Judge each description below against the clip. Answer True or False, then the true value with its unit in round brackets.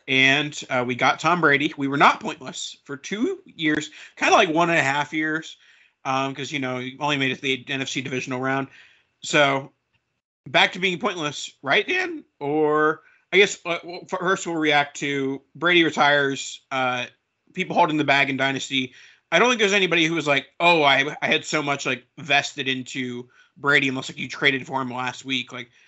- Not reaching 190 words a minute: False (195 wpm)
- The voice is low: False (145 Hz)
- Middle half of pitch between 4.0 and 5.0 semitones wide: False (3.3 semitones)